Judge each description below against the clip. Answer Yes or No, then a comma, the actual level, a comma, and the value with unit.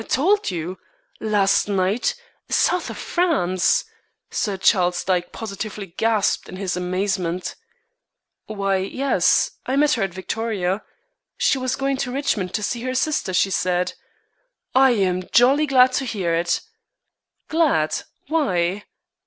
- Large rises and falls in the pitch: Yes, wide, 6.0 semitones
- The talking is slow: Yes, slow, 130 wpm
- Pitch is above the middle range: Yes, high, 205 Hz